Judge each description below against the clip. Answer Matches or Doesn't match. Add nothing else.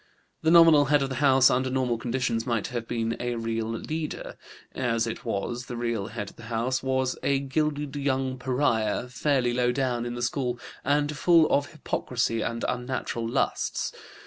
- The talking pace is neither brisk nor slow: Matches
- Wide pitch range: Doesn't match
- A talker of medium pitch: Doesn't match